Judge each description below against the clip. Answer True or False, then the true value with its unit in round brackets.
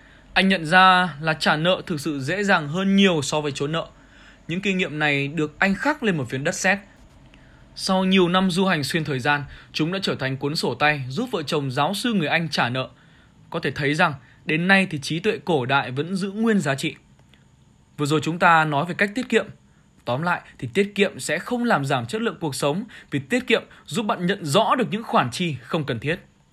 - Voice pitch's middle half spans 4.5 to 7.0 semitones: True (4.8 semitones)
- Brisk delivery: False (235 wpm)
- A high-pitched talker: False (170 Hz)